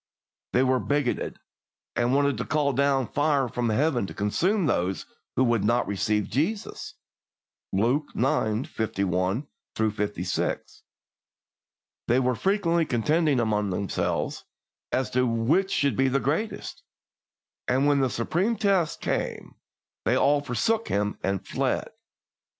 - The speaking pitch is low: Yes, low, 130 Hz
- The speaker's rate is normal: No, slow, 125 wpm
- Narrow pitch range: No, average, 5.1 semitones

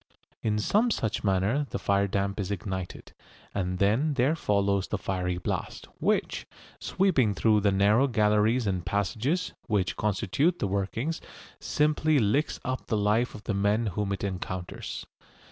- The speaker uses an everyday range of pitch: Yes, average, 4.1 semitones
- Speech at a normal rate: Yes, average, 150 wpm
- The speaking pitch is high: No, low, 105 Hz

